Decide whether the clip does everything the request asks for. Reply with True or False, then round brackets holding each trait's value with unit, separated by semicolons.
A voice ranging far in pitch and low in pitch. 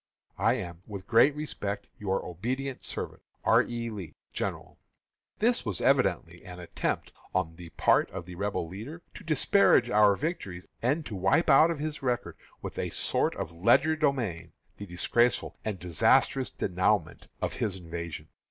True (7.1 semitones; 105 Hz)